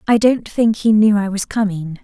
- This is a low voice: No, high, 210 Hz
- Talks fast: Yes, fast, 235 wpm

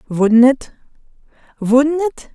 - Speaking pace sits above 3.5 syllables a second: No, 3.1 syllables/s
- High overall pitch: Yes, very high, 260 Hz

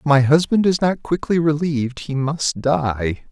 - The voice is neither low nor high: Yes, medium, 145 Hz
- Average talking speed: Yes, average, 180 wpm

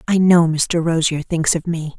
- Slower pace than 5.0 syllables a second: Yes, 4.4 syllables/s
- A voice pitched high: No, medium, 165 Hz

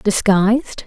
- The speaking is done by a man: No, female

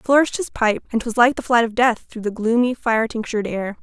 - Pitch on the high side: Yes, high, 230 Hz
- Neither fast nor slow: No, fast, 265 wpm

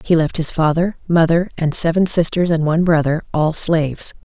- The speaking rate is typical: Yes, average, 180 wpm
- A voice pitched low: No, medium, 165 Hz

